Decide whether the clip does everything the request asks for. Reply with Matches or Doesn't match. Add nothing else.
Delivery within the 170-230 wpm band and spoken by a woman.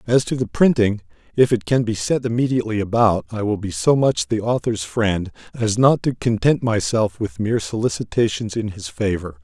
Doesn't match